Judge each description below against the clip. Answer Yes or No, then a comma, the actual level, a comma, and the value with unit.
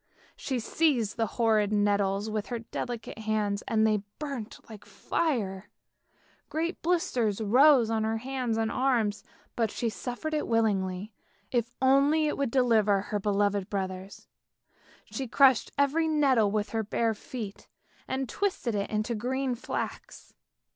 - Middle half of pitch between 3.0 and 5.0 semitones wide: Yes, average, 4.0 semitones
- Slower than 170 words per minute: Yes, average, 140 wpm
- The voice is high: Yes, high, 225 Hz